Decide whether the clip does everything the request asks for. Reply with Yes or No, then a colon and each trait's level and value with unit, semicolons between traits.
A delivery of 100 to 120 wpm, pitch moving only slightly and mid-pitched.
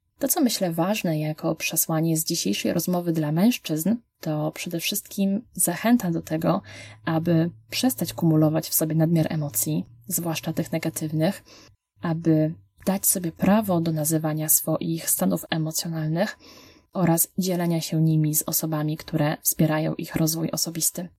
No: average, 135 wpm; narrow, 2.1 semitones; medium, 165 Hz